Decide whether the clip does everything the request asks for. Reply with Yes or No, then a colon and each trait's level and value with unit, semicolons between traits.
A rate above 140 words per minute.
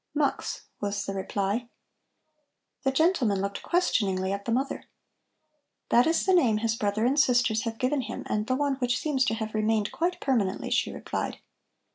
Yes: average, 170 wpm